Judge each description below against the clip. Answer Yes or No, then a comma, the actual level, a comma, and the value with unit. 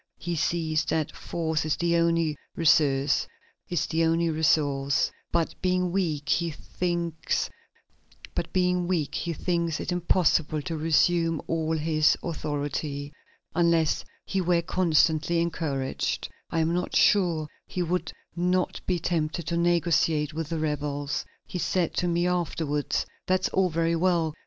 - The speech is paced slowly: Yes, slow, 120 wpm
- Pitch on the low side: No, medium, 165 Hz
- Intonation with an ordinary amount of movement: No, narrow, 2.0 semitones